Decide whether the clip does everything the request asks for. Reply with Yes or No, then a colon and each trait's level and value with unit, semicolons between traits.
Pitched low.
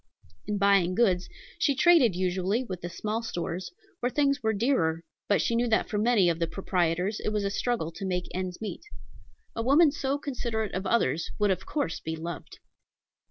No: high, 200 Hz